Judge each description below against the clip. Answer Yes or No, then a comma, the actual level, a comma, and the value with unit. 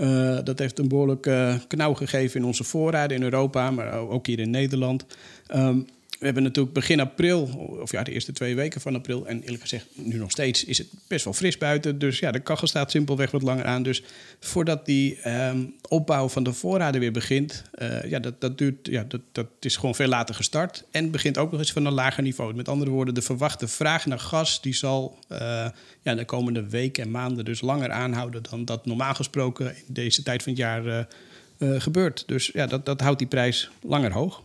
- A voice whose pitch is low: Yes, low, 130 Hz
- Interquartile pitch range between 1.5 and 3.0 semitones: Yes, narrow, 2.5 semitones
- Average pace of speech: No, fast, 220 wpm